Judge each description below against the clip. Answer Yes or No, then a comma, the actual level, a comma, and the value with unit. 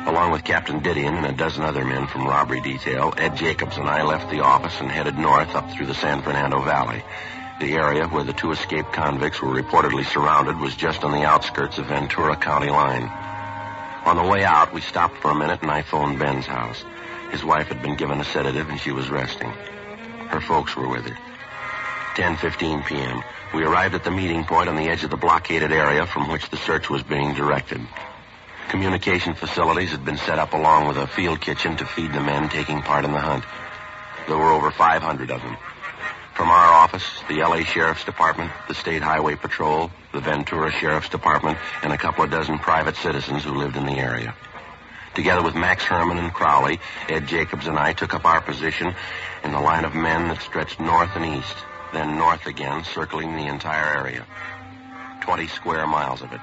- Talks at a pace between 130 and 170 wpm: No, average, 200 wpm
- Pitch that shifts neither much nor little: No, narrow, 2.3 semitones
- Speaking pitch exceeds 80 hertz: No, very low, 75 Hz